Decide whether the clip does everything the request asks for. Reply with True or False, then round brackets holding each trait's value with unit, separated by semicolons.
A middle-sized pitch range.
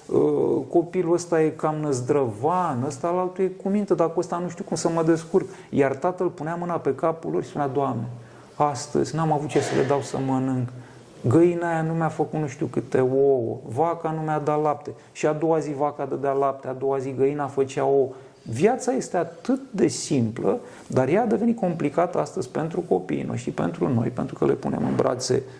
True (4.0 semitones)